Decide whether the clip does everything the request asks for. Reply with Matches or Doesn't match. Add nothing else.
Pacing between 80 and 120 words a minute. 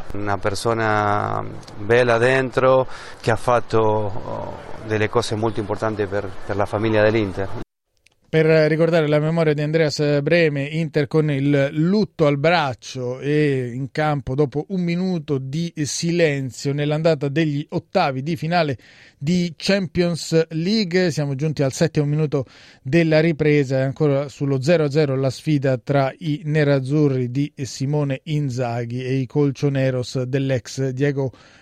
Doesn't match